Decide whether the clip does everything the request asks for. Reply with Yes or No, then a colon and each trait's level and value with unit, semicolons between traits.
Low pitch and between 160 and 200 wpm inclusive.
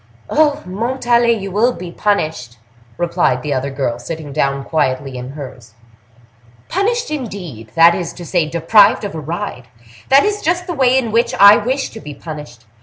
No: medium, 175 Hz; average, 170 wpm